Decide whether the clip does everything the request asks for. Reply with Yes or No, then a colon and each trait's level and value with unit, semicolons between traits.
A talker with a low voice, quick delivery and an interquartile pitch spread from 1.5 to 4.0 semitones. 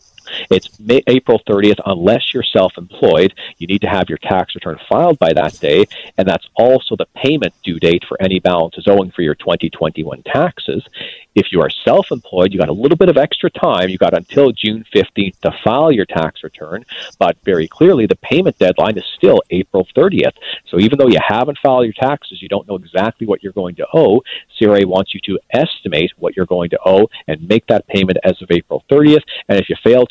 No: low, 100 Hz; fast, 210 wpm; average, 5.0 semitones